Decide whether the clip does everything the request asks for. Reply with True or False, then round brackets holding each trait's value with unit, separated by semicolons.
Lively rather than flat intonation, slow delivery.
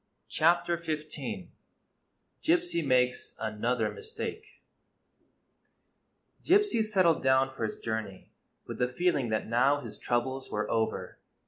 True (6.8 semitones; 120 wpm)